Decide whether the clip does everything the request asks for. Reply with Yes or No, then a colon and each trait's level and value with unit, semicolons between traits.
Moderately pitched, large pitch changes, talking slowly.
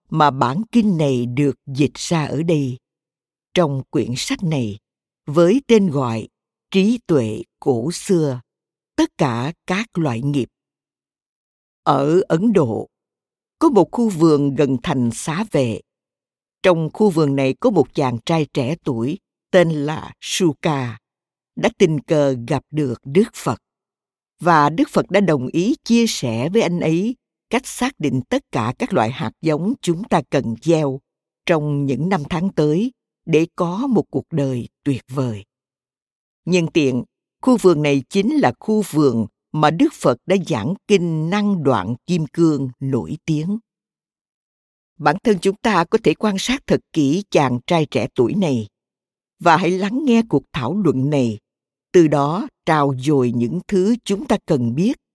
Yes: medium, 160 Hz; wide, 6.2 semitones; slow, 160 wpm